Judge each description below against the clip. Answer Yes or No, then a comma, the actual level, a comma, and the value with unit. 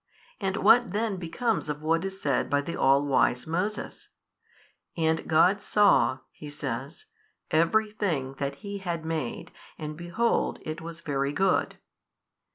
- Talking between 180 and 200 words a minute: No, average, 145 wpm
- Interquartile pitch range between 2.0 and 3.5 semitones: No, average, 5.2 semitones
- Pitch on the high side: No, medium, 165 Hz